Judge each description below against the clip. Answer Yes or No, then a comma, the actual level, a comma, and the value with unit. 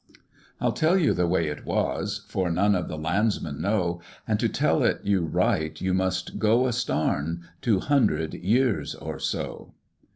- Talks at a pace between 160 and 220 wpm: Yes, average, 170 wpm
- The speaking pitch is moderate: No, very low, 95 Hz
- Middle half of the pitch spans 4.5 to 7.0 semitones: Yes, average, 5.1 semitones